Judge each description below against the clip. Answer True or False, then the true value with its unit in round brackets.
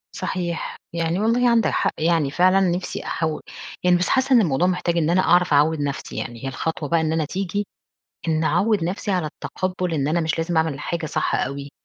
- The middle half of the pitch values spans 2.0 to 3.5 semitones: True (2.8 semitones)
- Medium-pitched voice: True (170 Hz)